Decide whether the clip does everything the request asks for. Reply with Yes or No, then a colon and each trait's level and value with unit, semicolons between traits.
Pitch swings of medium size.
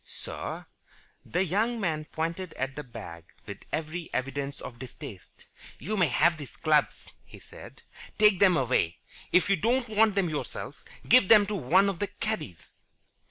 No: wide, 6.4 semitones